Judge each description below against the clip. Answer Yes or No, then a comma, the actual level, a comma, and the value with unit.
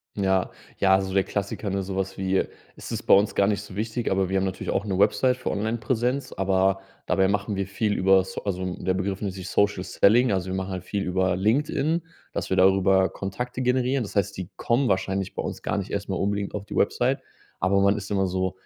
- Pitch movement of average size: No, narrow, 1.7 semitones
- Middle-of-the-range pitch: No, low, 100 Hz